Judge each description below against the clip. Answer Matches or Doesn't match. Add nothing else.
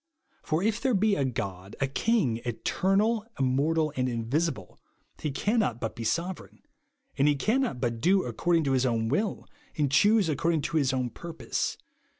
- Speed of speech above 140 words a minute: Matches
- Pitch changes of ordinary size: Doesn't match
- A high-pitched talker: Doesn't match